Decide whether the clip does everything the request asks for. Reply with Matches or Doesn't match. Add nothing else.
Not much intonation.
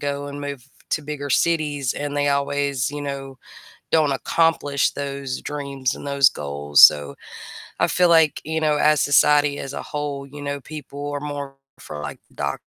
Matches